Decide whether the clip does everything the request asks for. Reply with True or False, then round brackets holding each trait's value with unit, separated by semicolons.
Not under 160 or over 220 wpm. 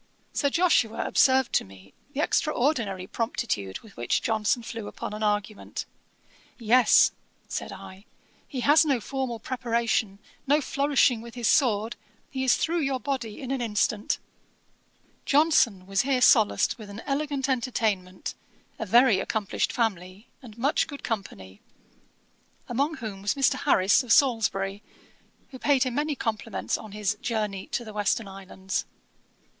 False (145 wpm)